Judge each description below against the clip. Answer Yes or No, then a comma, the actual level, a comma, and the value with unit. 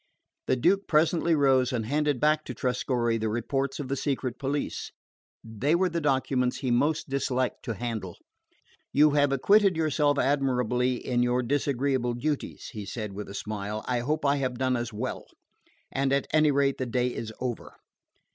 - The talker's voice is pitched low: Yes, low, 130 Hz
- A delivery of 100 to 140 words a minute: No, average, 170 wpm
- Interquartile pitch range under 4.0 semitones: Yes, average, 3.1 semitones